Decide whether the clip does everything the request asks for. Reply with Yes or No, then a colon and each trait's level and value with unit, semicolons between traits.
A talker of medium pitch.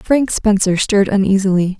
No: high, 200 Hz